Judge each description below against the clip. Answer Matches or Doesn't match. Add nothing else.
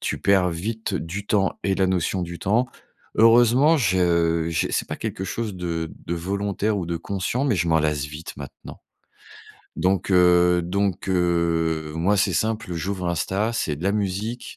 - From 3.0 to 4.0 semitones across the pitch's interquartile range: Matches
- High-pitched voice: Doesn't match